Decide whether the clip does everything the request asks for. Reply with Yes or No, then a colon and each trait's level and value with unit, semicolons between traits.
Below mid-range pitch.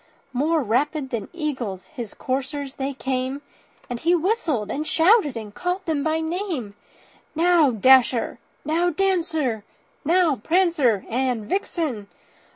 No: very high, 290 Hz